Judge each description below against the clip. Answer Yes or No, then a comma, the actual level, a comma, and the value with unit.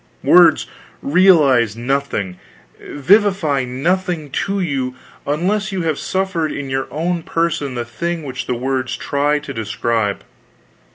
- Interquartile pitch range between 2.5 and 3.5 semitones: No, average, 5.1 semitones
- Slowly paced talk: Yes, slow, 125 wpm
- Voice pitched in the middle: Yes, medium, 145 Hz